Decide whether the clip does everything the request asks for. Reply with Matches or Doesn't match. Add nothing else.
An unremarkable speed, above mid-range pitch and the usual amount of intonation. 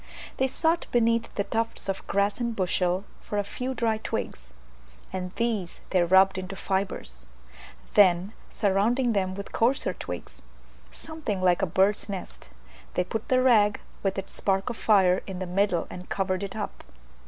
Matches